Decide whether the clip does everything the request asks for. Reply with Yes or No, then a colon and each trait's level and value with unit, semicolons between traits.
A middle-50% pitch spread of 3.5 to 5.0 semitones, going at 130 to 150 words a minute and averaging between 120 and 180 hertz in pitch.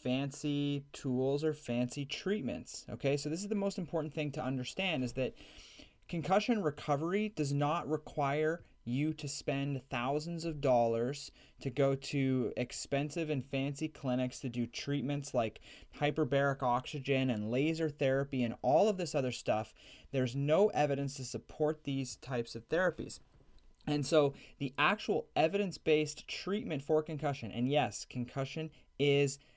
No: average, 3.0 semitones; average, 145 wpm; medium, 140 Hz